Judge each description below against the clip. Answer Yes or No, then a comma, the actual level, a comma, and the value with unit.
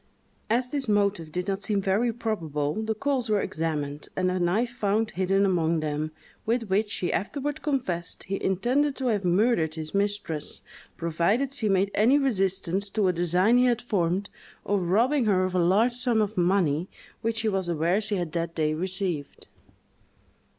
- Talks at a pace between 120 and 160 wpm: No, average, 175 wpm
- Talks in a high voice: Yes, high, 195 Hz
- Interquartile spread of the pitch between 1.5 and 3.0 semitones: No, average, 4.5 semitones